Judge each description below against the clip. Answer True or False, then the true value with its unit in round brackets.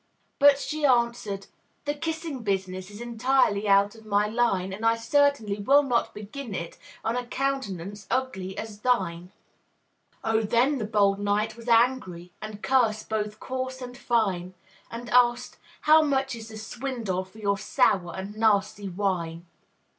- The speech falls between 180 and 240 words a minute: False (155 wpm)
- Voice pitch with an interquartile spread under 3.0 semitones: False (4.0 semitones)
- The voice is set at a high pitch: True (220 Hz)